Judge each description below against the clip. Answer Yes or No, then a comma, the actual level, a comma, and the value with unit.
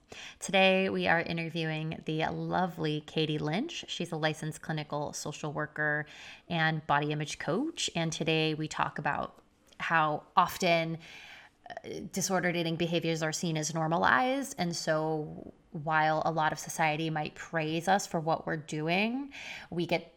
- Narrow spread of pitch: Yes, narrow, 1.9 semitones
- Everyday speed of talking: Yes, average, 145 wpm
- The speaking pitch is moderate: Yes, medium, 165 Hz